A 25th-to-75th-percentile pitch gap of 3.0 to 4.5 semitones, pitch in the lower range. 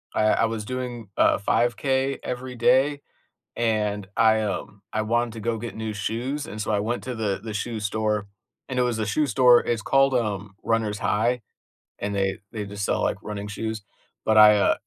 No: narrow, 2.6 semitones; low, 110 Hz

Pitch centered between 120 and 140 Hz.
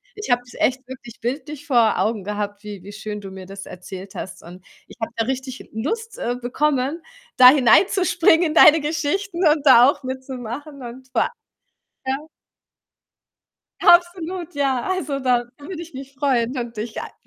No: very high, 260 Hz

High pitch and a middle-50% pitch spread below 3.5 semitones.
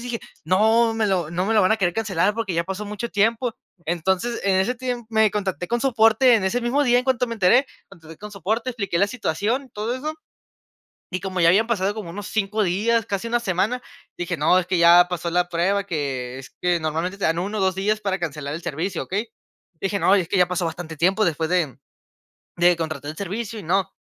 No: high, 195 Hz; average, 4.2 semitones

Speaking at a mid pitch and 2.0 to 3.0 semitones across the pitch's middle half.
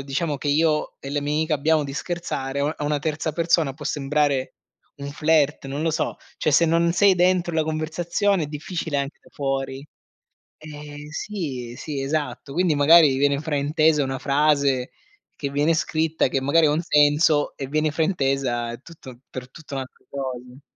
Yes: medium, 150 Hz; narrow, 2.5 semitones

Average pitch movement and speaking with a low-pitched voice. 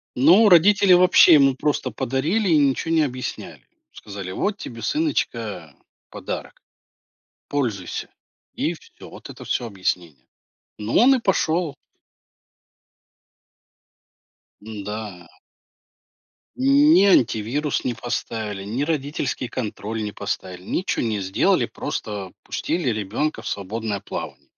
No: wide, 7.9 semitones; low, 125 Hz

